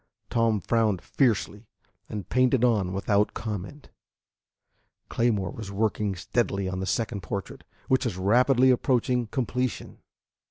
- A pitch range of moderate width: Yes, average, 3.9 semitones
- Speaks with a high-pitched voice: No, low, 110 Hz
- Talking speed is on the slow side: Yes, slow, 120 wpm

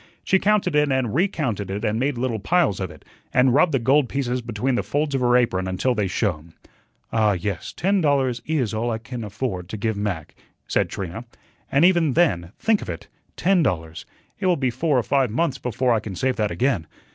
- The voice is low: Yes, low, 125 Hz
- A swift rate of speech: Yes, fast, 215 wpm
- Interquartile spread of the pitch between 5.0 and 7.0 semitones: Yes, wide, 5.5 semitones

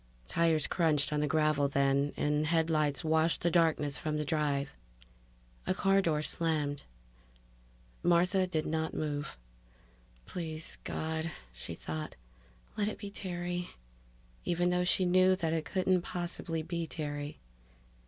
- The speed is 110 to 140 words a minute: Yes, slow, 135 wpm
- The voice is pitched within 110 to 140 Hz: No, medium, 160 Hz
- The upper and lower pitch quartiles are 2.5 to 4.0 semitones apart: Yes, average, 2.8 semitones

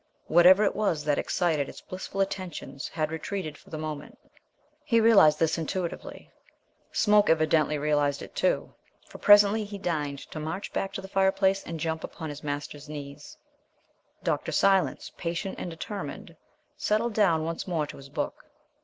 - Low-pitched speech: No, medium, 165 Hz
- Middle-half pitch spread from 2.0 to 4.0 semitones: No, average, 4.4 semitones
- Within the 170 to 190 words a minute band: No, average, 160 wpm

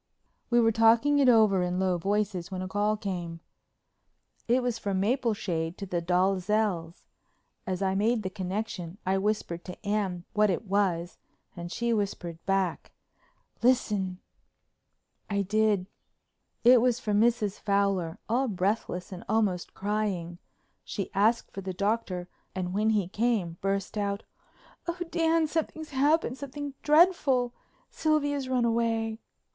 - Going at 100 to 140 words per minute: Yes, slow, 135 wpm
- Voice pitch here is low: No, high, 205 Hz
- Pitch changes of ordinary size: Yes, average, 4.0 semitones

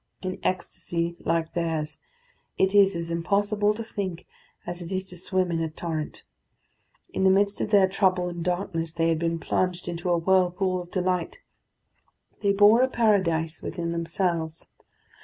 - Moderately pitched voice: Yes, medium, 180 Hz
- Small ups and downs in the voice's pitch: Yes, narrow, 2.3 semitones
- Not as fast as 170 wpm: Yes, average, 160 wpm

